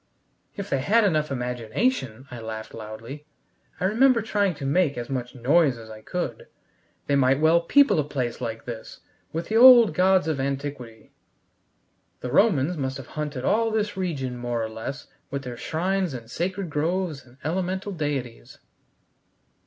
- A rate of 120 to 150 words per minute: No, average, 160 wpm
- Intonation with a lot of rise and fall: Yes, wide, 7.1 semitones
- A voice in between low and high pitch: Yes, medium, 145 Hz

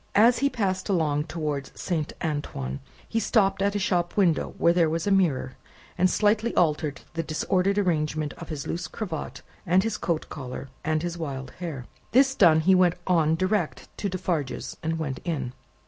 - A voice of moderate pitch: Yes, medium, 170 Hz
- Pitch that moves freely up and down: No, average, 3.9 semitones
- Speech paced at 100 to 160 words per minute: No, average, 180 wpm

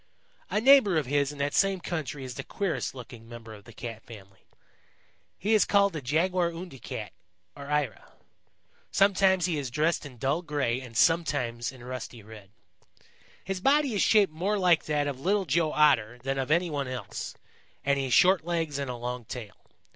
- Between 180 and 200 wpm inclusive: Yes, average, 185 wpm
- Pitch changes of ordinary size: No, wide, 6.3 semitones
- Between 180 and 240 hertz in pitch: No, medium, 145 Hz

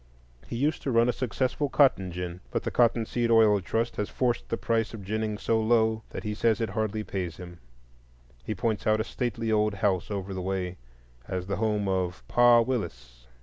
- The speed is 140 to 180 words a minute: No, average, 200 wpm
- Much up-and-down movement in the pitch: No, average, 3.4 semitones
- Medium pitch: No, low, 110 Hz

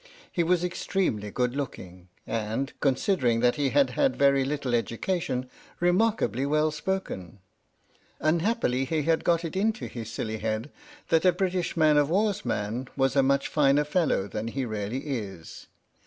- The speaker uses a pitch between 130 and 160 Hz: Yes, medium, 140 Hz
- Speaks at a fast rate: No, average, 155 wpm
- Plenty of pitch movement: Yes, wide, 6.8 semitones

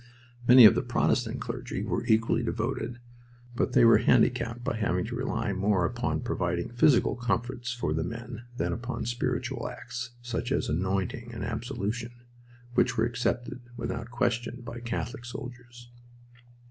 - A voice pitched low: Yes, low, 120 Hz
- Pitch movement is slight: Yes, narrow, 1.3 semitones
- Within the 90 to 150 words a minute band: Yes, average, 145 wpm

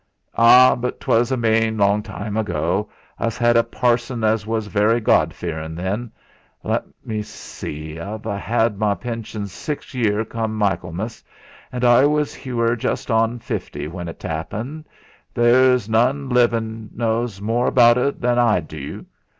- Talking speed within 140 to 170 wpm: Yes, average, 150 wpm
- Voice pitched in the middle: No, low, 115 Hz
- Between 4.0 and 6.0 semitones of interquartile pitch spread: No, average, 2.8 semitones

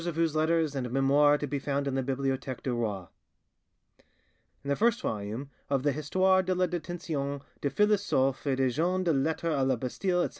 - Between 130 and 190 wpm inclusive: No, average, 200 wpm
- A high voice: No, medium, 140 Hz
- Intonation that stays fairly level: No, average, 3.9 semitones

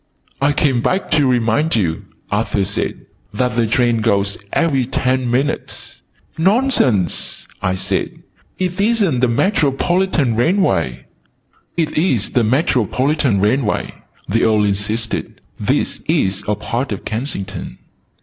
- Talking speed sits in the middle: No, slow, 125 wpm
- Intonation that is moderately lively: No, wide, 6.1 semitones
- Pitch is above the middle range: No, low, 125 Hz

